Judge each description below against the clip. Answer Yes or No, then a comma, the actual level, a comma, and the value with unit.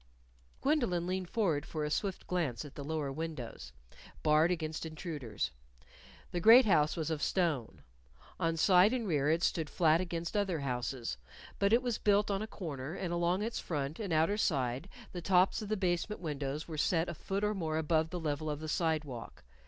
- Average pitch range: Yes, average, 3.9 semitones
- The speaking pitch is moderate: Yes, medium, 165 Hz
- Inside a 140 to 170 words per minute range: No, average, 190 wpm